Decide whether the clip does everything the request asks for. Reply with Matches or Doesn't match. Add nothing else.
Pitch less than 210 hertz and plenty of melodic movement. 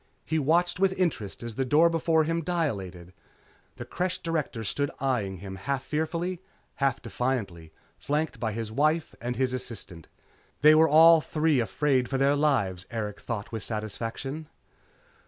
Matches